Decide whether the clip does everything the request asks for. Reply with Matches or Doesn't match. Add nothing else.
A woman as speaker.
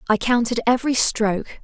Matches